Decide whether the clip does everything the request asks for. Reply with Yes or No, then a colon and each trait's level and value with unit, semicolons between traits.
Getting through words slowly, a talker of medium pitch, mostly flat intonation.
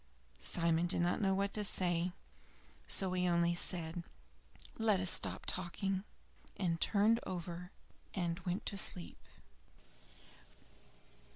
Yes: slow, 115 wpm; medium, 180 Hz; narrow, 2.1 semitones